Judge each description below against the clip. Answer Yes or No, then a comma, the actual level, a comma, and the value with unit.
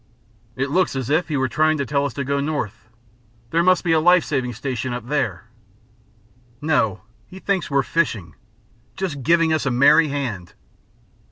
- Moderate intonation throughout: Yes, average, 4.2 semitones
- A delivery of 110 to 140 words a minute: No, average, 175 wpm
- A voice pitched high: No, medium, 140 Hz